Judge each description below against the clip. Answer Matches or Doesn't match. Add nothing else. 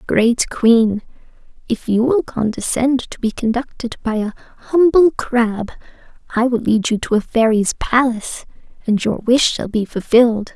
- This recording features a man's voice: Doesn't match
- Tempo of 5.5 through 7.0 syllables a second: Doesn't match